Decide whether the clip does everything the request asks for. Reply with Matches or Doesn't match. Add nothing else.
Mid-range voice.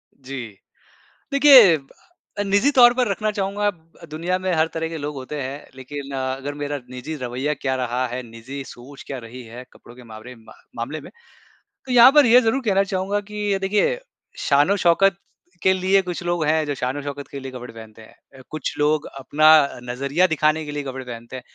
Matches